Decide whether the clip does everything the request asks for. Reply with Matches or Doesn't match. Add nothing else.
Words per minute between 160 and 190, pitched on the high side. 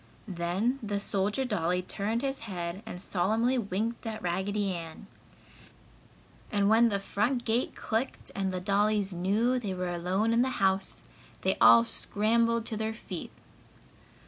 Doesn't match